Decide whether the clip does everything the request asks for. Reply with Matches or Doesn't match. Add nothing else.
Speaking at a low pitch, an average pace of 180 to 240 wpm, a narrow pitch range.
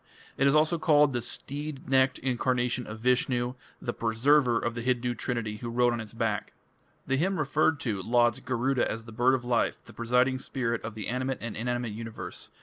Matches